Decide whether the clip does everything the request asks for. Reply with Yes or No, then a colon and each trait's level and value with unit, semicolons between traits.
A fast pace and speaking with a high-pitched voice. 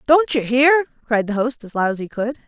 Yes: fast, 265 wpm; very high, 250 Hz